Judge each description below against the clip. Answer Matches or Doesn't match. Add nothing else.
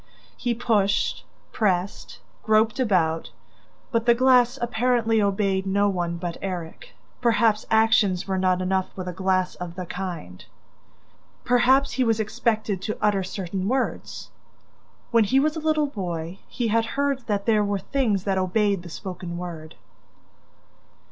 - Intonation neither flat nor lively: Matches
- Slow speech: Doesn't match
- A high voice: Matches